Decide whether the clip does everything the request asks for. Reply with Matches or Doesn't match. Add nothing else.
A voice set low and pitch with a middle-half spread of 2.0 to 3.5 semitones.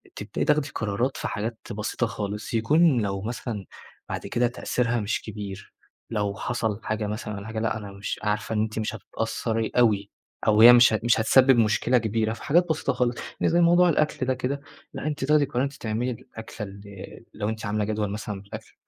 Matches